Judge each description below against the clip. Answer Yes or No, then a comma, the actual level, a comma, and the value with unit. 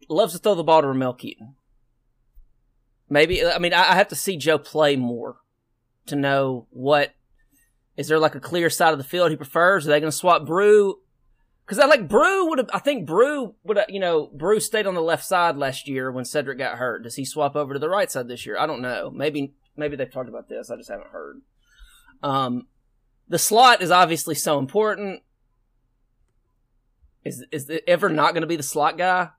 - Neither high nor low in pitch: Yes, medium, 150 Hz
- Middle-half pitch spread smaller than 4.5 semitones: No, wide, 5.5 semitones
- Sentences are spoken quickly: Yes, fast, 210 wpm